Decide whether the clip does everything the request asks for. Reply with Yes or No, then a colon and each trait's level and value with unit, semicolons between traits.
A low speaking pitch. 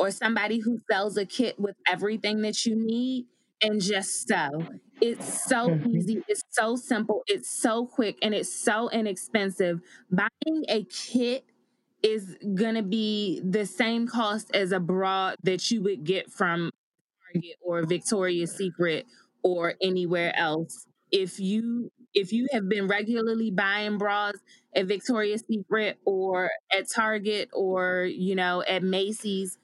No: high, 205 Hz